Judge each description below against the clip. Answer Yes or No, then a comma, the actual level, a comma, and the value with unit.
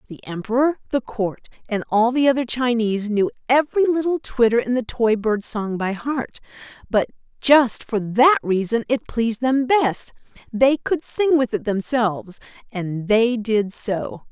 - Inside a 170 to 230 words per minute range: No, average, 160 wpm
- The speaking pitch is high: Yes, high, 235 Hz